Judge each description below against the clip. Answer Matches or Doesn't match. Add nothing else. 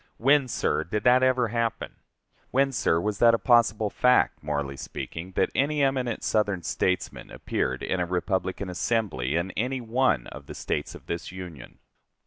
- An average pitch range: Doesn't match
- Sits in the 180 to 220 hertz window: Doesn't match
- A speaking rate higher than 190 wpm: Doesn't match